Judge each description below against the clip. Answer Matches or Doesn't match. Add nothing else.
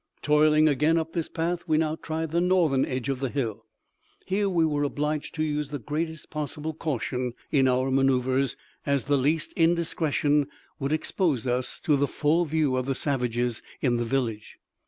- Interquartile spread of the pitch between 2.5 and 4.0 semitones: Matches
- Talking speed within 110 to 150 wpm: Doesn't match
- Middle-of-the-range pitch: Matches